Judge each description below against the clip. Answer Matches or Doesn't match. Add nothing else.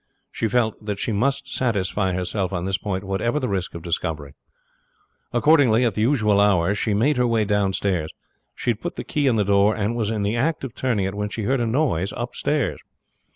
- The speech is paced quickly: Matches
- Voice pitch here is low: Matches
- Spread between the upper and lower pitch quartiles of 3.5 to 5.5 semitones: Matches